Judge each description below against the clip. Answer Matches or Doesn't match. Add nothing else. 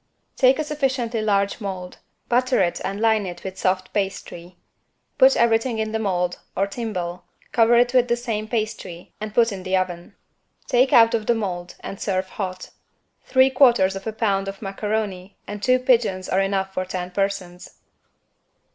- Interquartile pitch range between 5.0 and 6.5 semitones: Doesn't match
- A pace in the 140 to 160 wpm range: Doesn't match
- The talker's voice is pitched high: Matches